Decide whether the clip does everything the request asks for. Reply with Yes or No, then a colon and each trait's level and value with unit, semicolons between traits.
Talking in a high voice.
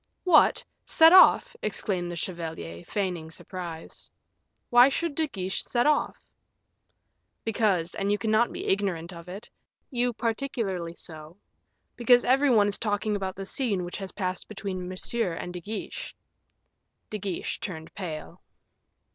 Yes: high, 195 Hz